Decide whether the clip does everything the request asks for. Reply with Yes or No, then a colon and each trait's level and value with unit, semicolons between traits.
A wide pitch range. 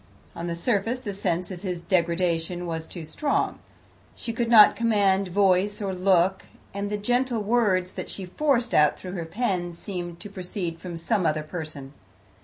No: average, 3.4 semitones